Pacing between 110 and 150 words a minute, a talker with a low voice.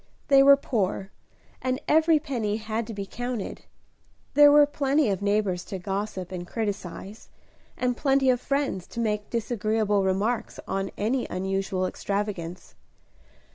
No: slow, 135 wpm; high, 215 Hz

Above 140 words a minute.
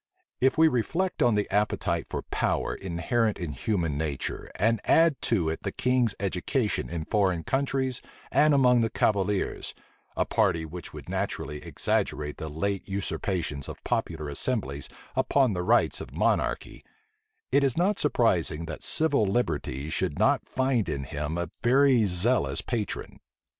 Yes: average, 150 wpm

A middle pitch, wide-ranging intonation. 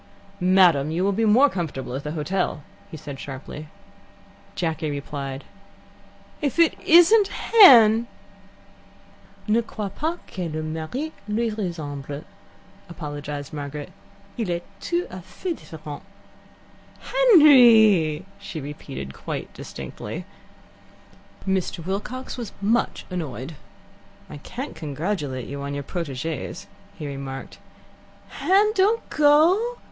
Yes: medium, 175 Hz; wide, 8.5 semitones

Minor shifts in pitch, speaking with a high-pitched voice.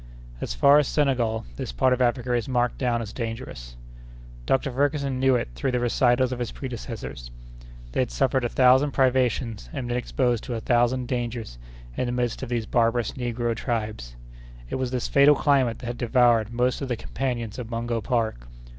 No: narrow, 2.0 semitones; low, 120 Hz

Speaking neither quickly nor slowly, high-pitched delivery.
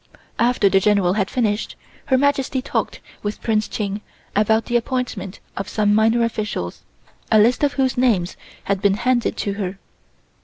Yes: average, 160 wpm; high, 215 Hz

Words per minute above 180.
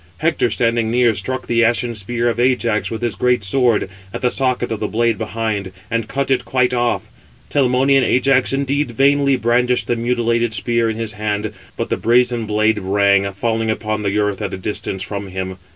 Yes: average, 190 wpm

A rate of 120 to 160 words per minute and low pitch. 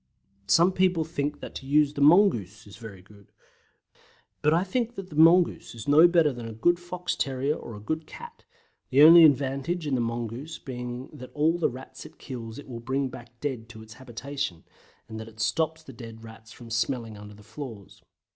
No: fast, 205 wpm; low, 130 Hz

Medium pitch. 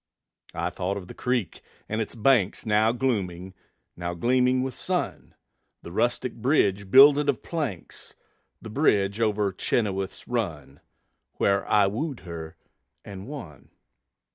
No: low, 105 Hz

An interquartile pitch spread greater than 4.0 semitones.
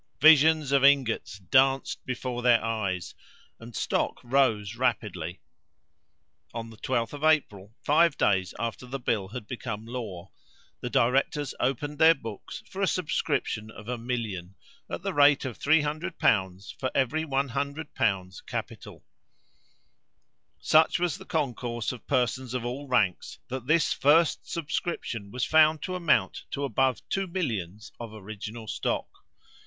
Yes: average, 4.9 semitones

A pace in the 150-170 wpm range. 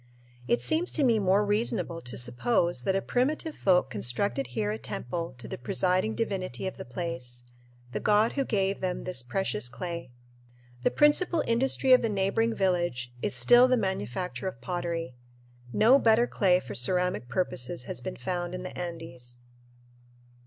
Yes: average, 165 wpm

